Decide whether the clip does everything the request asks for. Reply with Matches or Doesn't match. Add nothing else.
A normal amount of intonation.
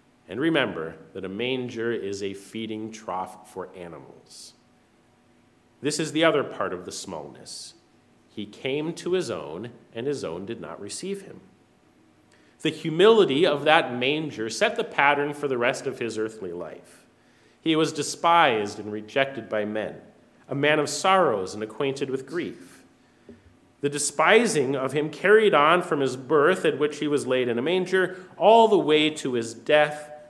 Doesn't match